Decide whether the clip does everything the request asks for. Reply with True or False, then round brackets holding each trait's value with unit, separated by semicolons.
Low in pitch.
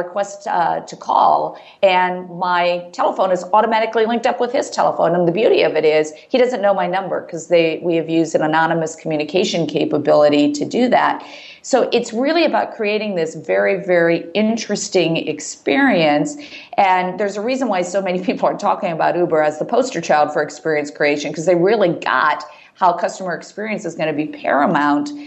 False (180 Hz)